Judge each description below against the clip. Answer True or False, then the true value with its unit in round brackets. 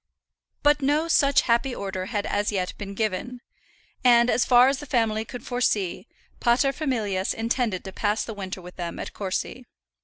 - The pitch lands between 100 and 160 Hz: False (225 Hz)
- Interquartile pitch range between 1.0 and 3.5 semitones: False (4.2 semitones)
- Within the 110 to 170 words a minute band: True (165 wpm)